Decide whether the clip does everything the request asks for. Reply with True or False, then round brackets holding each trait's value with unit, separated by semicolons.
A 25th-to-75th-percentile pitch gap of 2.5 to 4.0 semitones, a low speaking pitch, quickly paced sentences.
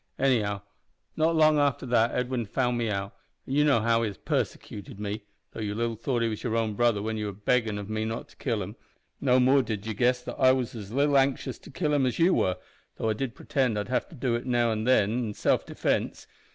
True (3.2 semitones; 120 Hz; 245 wpm)